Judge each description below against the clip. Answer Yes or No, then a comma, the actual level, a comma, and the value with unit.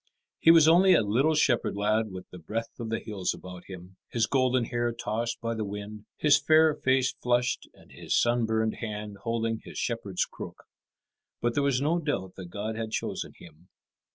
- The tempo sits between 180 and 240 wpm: Yes, average, 185 wpm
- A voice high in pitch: No, low, 115 Hz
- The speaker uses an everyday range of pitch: Yes, average, 3.8 semitones